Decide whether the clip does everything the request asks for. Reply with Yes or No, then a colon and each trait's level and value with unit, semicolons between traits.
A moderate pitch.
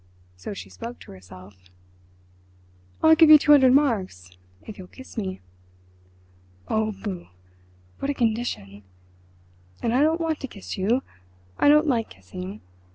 No: high, 215 Hz